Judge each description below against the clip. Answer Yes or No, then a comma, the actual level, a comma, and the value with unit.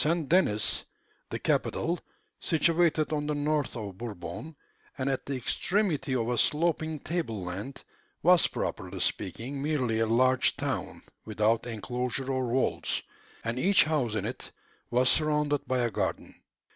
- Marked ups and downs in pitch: No, average, 5.0 semitones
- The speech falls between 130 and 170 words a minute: Yes, average, 145 wpm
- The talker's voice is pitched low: Yes, low, 130 Hz